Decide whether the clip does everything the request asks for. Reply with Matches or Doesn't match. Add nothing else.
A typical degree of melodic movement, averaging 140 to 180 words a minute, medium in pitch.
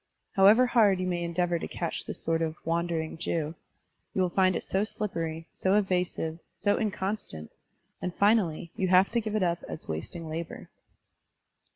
Matches